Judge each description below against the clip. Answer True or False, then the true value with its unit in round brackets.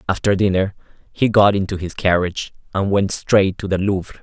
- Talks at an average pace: True (185 wpm)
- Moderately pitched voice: False (95 Hz)